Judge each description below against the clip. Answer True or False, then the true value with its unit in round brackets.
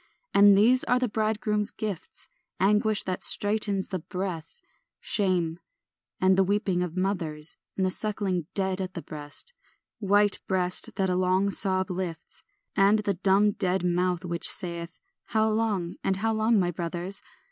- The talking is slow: False (155 wpm)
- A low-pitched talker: False (190 Hz)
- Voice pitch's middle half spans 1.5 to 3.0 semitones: True (2.5 semitones)